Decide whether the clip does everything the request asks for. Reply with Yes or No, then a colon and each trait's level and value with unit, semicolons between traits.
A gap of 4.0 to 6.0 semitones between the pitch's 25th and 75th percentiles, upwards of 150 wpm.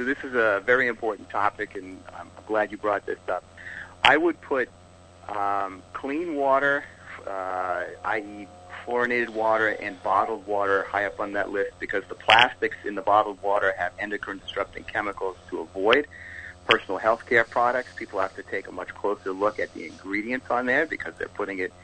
No: average, 3.2 semitones; average, 180 wpm